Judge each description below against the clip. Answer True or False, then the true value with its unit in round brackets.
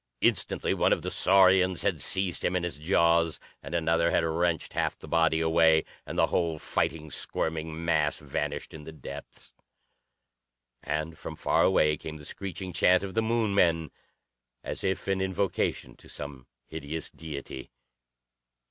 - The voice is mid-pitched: False (80 Hz)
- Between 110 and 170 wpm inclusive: True (155 wpm)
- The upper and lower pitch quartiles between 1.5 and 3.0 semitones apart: True (2.7 semitones)